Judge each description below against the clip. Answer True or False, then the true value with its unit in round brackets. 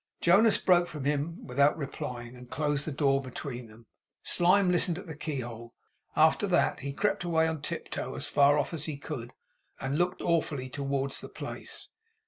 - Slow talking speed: False (175 wpm)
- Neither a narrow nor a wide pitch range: True (3.7 semitones)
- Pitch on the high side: False (145 Hz)